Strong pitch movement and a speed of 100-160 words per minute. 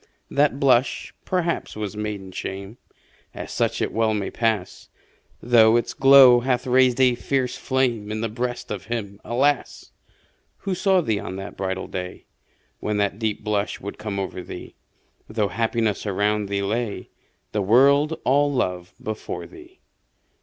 No: average, 4.2 semitones; average, 155 wpm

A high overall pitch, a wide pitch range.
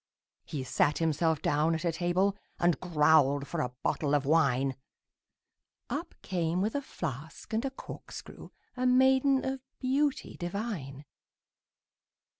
No: medium, 170 Hz; wide, 8.3 semitones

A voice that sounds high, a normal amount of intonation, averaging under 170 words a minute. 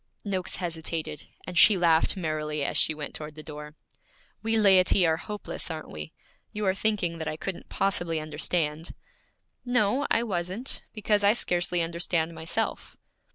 No: medium, 170 Hz; average, 3.9 semitones; average, 155 wpm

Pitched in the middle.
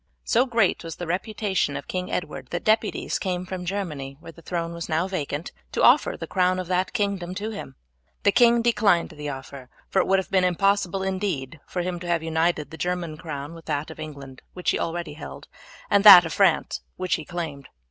Yes: medium, 175 Hz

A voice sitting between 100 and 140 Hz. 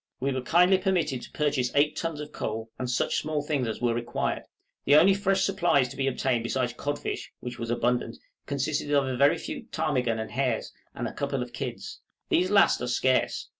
Yes: low, 135 Hz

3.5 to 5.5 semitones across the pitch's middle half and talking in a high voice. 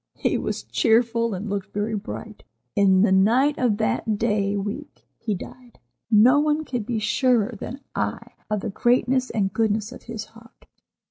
No: average, 3.0 semitones; high, 225 Hz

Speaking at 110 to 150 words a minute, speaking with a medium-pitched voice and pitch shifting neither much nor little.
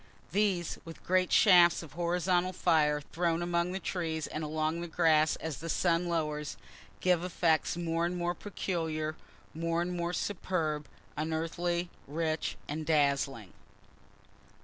No: slow, 135 wpm; medium, 165 Hz; narrow, 2.0 semitones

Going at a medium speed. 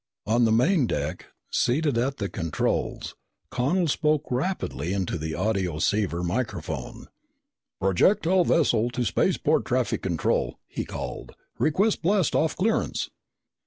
No: slow, 120 wpm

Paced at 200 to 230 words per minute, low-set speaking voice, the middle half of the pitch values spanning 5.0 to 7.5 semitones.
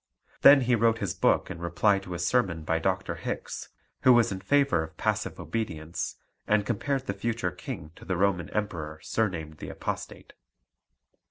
No: average, 170 wpm; very low, 95 Hz; average, 5.3 semitones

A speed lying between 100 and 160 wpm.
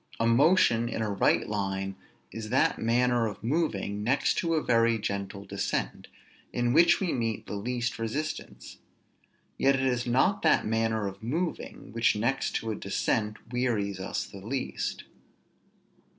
Yes: average, 150 wpm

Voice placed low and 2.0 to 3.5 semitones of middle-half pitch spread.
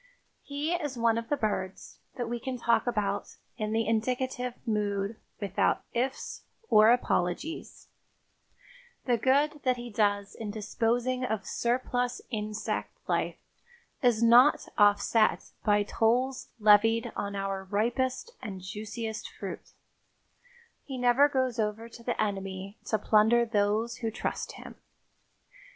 No: high, 225 Hz; average, 3.1 semitones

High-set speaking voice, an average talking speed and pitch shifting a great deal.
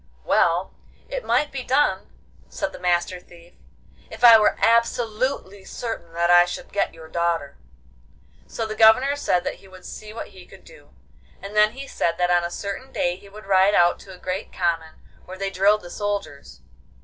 No: high, 195 Hz; average, 190 wpm; average, 4.1 semitones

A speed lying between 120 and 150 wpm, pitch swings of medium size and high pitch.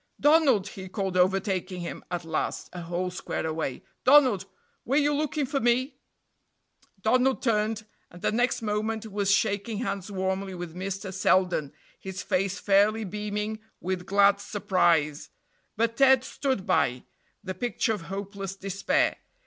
Yes: average, 140 wpm; average, 3.3 semitones; high, 200 Hz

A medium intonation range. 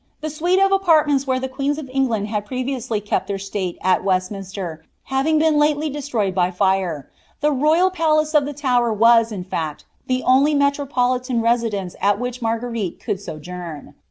No: wide, 6.6 semitones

